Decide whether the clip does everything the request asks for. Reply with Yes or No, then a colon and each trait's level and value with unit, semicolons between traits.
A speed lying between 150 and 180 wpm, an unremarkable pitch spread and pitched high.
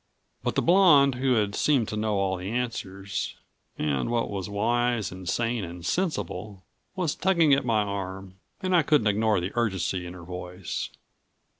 No: average, 165 wpm; average, 4.8 semitones; low, 105 Hz